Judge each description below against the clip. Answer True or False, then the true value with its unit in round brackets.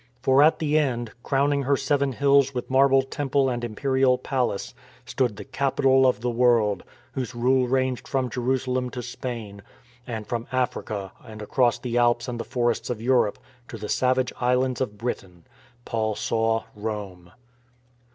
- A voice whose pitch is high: False (125 Hz)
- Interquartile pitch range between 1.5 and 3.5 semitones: True (2.7 semitones)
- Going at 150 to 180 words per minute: True (160 wpm)